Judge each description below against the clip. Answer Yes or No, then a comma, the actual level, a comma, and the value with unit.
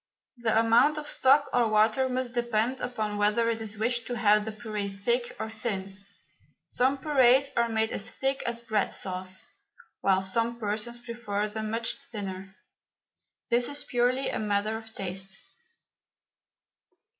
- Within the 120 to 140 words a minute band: No, average, 150 wpm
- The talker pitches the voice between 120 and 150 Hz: No, high, 225 Hz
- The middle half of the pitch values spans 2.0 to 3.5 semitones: Yes, narrow, 2.6 semitones